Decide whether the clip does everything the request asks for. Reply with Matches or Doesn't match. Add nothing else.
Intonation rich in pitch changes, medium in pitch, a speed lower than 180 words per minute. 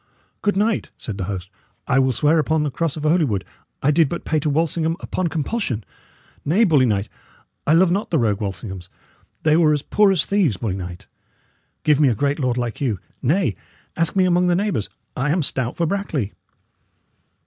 Doesn't match